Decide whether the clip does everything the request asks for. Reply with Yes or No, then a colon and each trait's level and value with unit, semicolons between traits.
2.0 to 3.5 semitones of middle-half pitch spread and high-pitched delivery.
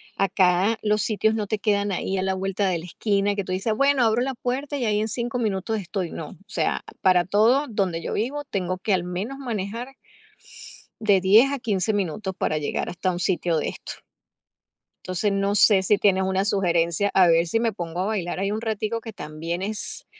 Yes: average, 3.1 semitones; high, 200 Hz